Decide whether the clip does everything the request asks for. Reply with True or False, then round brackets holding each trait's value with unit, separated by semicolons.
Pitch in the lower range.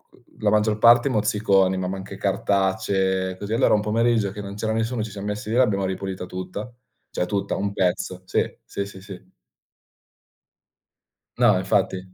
True (100 Hz)